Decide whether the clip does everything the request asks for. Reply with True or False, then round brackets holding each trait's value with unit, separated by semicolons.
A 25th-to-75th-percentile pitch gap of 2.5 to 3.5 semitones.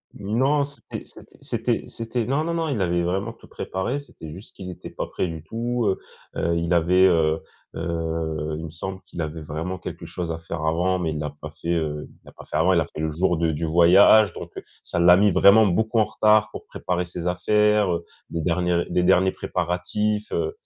False (4.3 semitones)